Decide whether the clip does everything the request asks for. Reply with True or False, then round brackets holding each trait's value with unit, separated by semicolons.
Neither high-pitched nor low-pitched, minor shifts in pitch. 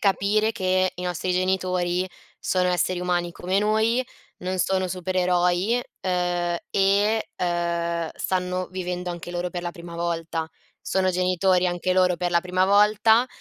True (180 Hz; 1.3 semitones)